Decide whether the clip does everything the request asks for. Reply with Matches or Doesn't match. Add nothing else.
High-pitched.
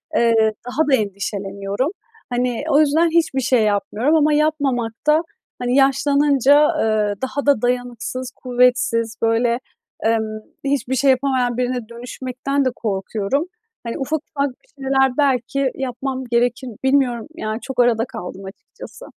Matches